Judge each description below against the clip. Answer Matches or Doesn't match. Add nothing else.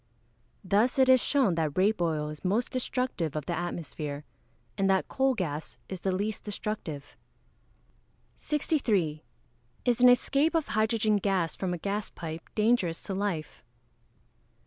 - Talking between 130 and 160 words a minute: Matches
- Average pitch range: Doesn't match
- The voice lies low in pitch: Doesn't match